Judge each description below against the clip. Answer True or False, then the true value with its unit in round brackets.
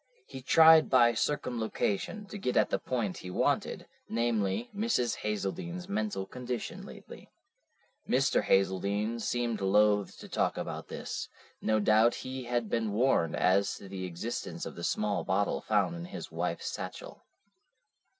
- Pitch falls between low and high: False (115 Hz)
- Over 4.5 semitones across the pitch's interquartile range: False (4.2 semitones)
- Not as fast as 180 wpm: True (145 wpm)